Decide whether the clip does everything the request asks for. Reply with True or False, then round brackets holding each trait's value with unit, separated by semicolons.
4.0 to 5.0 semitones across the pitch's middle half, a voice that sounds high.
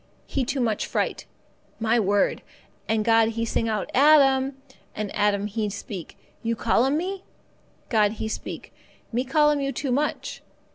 True (4.3 semitones; 230 Hz)